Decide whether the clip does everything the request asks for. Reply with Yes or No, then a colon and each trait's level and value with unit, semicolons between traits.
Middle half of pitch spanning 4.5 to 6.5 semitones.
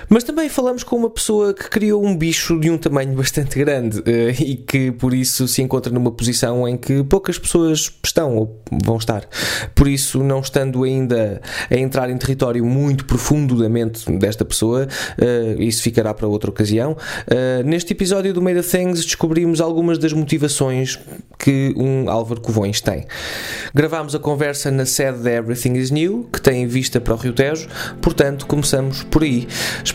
Yes: average, 4.8 semitones